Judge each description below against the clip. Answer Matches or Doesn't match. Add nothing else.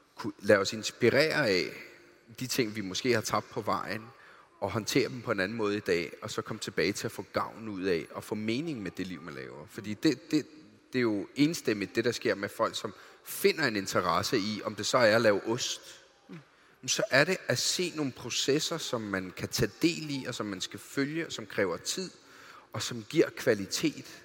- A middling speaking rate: Doesn't match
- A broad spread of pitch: Matches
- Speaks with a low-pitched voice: Matches